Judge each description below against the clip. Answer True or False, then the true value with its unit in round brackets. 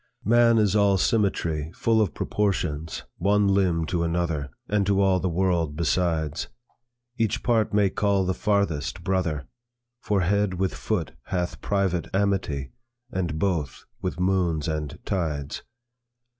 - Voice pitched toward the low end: True (95 Hz)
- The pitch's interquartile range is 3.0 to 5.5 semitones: True (3.7 semitones)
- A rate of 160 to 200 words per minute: False (135 wpm)